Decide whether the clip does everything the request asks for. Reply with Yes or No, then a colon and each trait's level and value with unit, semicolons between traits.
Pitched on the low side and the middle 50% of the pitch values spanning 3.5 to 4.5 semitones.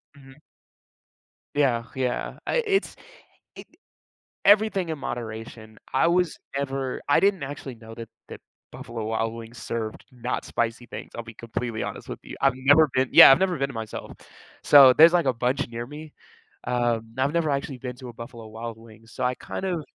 Yes: low, 125 Hz; average, 3.9 semitones